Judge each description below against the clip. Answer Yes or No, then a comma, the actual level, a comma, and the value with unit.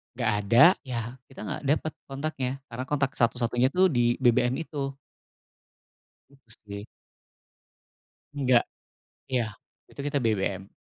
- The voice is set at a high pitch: No, low, 125 Hz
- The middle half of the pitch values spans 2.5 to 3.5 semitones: Yes, average, 3.1 semitones